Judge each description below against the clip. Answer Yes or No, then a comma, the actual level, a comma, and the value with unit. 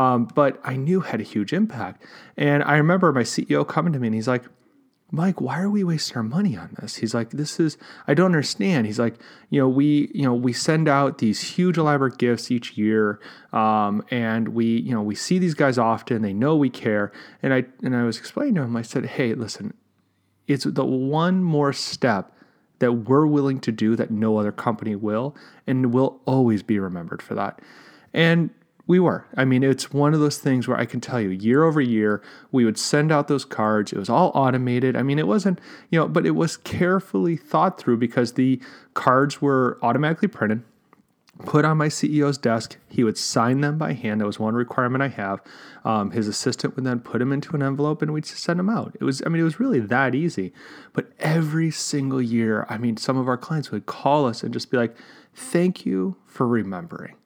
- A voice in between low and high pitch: No, low, 130 Hz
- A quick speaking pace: Yes, fast, 220 wpm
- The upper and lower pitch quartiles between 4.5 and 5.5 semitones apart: Yes, average, 4.9 semitones